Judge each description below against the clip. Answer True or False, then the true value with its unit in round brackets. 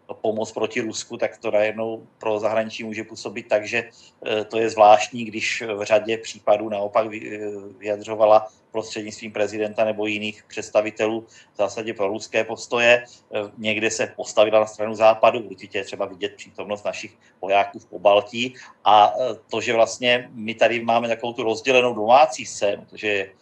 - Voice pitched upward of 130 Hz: False (110 Hz)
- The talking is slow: False (150 wpm)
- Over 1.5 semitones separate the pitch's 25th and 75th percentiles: False (1.2 semitones)